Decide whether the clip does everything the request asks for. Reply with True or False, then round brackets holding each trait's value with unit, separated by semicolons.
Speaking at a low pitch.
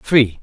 True (115 Hz)